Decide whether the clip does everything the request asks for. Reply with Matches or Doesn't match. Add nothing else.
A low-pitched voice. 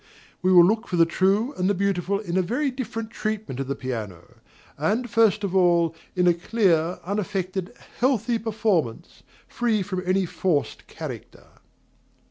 Doesn't match